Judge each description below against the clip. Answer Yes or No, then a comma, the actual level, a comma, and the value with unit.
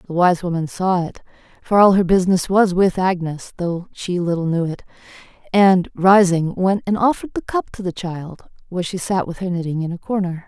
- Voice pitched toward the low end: No, medium, 180 Hz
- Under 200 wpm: No, fast, 205 wpm